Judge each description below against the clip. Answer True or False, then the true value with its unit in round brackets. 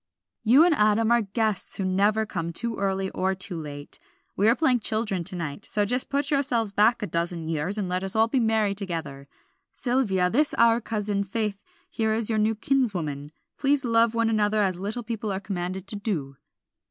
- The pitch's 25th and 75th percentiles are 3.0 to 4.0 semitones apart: True (3.5 semitones)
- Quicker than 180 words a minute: True (195 wpm)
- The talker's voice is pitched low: False (210 Hz)